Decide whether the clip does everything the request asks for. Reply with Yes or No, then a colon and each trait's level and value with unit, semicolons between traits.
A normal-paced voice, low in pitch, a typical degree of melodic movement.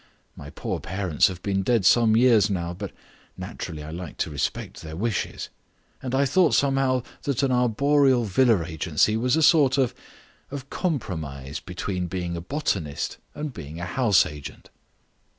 No: average, 160 wpm; low, 105 Hz; wide, 7.3 semitones